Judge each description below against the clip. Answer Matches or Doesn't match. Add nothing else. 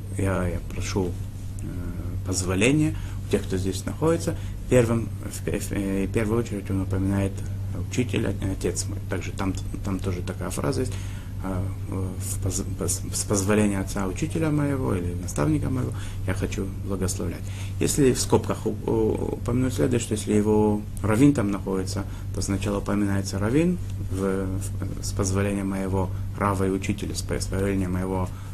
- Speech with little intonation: Matches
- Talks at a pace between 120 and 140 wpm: Matches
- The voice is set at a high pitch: Doesn't match